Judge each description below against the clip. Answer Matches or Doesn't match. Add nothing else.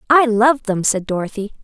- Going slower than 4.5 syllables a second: Doesn't match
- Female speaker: Matches